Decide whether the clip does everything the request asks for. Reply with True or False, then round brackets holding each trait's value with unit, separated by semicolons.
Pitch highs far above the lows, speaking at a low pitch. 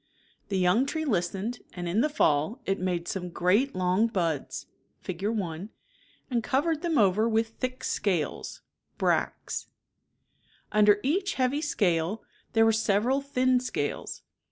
False (5.8 semitones; 215 Hz)